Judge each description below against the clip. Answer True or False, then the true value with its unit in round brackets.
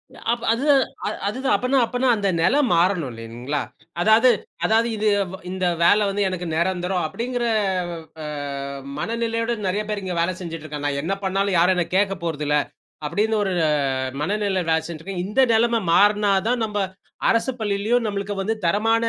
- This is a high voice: True (200 Hz)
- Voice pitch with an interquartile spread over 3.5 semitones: True (4.2 semitones)